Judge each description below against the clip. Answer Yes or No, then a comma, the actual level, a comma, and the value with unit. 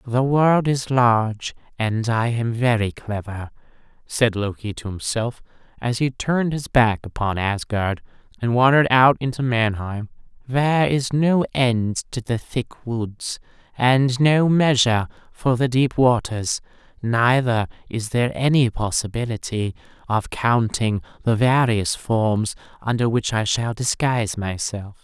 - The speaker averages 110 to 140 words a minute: Yes, slow, 135 wpm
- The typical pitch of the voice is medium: No, low, 120 Hz